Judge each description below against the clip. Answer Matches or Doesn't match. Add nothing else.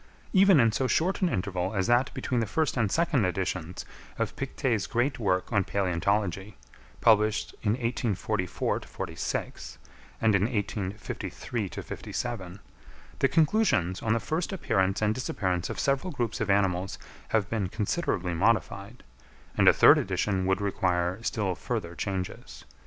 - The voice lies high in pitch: Doesn't match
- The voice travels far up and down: Doesn't match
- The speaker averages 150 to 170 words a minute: Doesn't match